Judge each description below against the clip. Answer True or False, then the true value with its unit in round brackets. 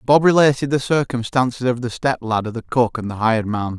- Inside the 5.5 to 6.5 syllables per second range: True (5.7 syllables/s)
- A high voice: False (125 Hz)